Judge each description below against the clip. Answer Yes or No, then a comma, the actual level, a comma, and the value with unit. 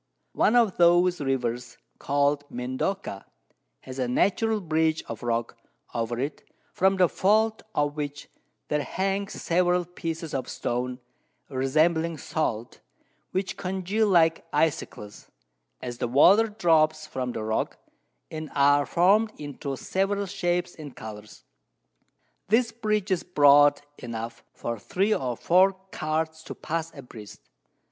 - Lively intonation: Yes, wide, 6.2 semitones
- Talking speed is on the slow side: Yes, slow, 130 wpm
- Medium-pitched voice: Yes, medium, 155 Hz